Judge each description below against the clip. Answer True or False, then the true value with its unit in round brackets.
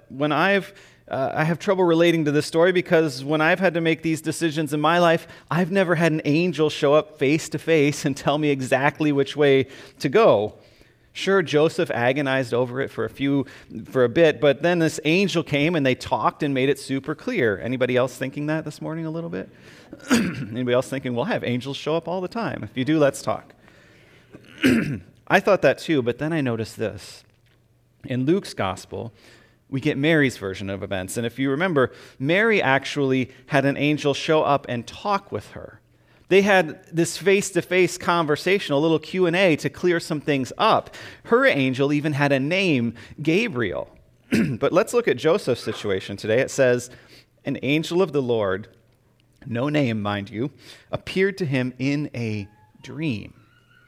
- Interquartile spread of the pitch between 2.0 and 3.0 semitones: False (4.6 semitones)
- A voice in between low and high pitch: True (145 Hz)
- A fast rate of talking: False (185 wpm)